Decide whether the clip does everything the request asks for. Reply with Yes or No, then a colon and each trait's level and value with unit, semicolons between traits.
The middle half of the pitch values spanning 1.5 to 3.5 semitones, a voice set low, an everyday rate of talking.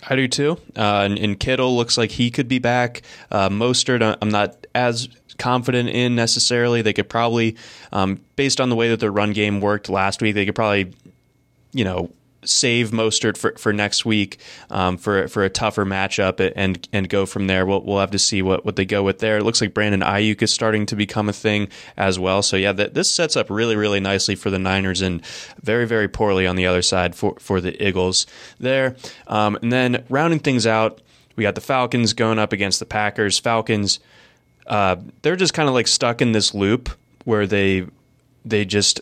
No: average, 3.2 semitones; low, 105 Hz; fast, 210 wpm